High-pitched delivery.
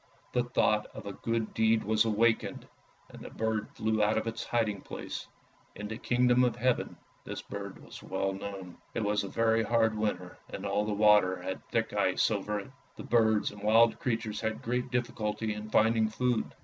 No: low, 110 Hz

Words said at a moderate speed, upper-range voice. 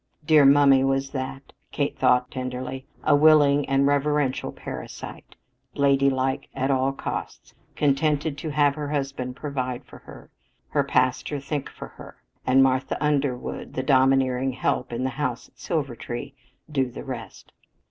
No: average, 145 wpm; low, 135 Hz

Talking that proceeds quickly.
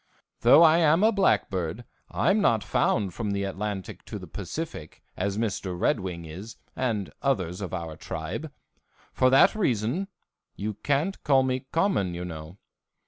No: average, 155 wpm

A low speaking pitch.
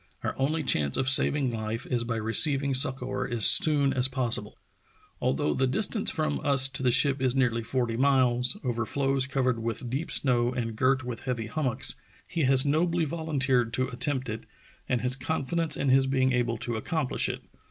Yes: low, 130 Hz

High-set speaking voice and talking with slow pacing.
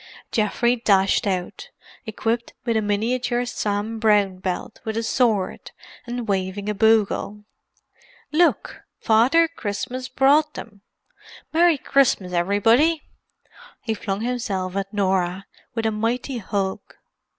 Yes: high, 220 Hz; slow, 115 wpm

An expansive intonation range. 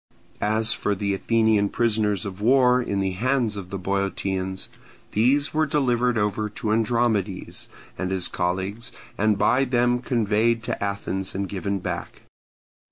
No: average, 3.4 semitones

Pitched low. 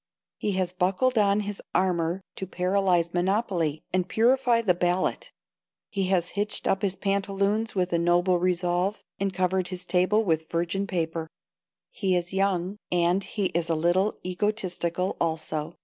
No: medium, 185 Hz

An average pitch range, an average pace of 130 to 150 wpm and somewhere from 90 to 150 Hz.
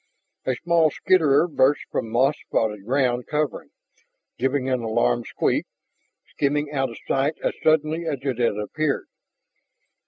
Yes: average, 3.8 semitones; slow, 135 wpm; low, 135 Hz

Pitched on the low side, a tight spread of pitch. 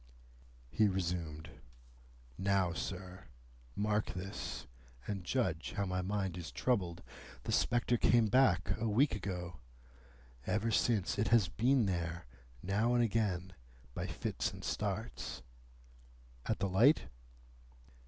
No: low, 100 Hz; average, 3.7 semitones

